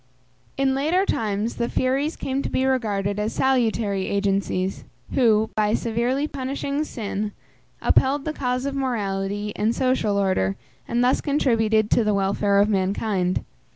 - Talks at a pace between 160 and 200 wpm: No, average, 145 wpm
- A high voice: Yes, high, 225 Hz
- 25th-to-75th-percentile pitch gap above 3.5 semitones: Yes, average, 4.6 semitones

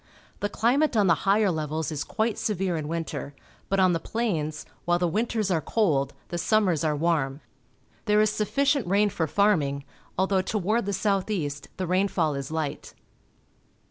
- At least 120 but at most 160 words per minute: No, average, 175 wpm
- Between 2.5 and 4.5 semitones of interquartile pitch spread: No, average, 5.1 semitones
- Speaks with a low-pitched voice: No, medium, 185 Hz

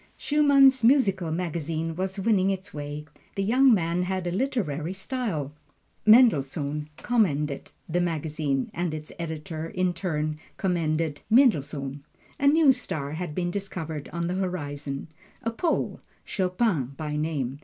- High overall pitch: No, medium, 170 Hz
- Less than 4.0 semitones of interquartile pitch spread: No, average, 4.7 semitones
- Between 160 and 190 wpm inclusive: No, slow, 135 wpm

